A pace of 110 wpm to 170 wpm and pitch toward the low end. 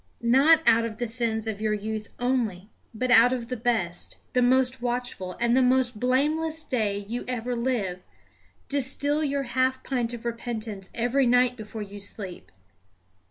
No: average, 160 wpm; high, 240 Hz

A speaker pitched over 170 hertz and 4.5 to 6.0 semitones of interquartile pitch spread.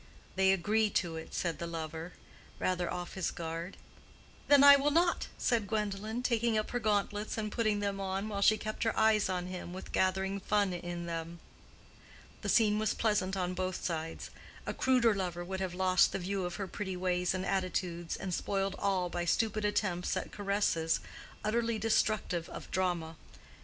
No: high, 190 Hz; average, 3.1 semitones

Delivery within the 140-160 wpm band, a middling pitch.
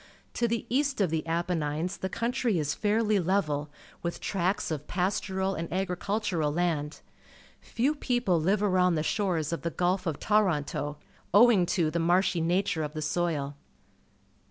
Yes: average, 155 wpm; medium, 180 Hz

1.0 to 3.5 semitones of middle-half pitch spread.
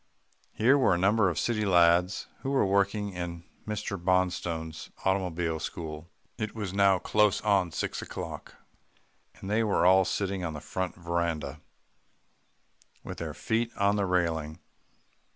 Yes: average, 3.1 semitones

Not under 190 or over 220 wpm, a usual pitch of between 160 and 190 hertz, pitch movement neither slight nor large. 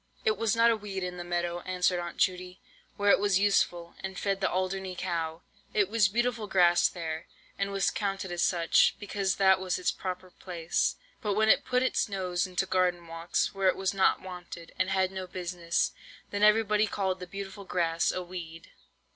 No: average, 195 wpm; medium, 185 Hz; narrow, 2.1 semitones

